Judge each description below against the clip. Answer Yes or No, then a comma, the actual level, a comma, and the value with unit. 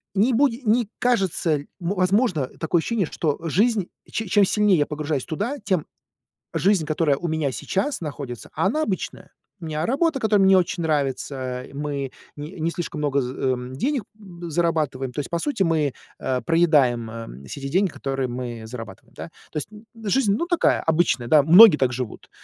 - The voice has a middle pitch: Yes, medium, 160 Hz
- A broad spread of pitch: Yes, wide, 6.6 semitones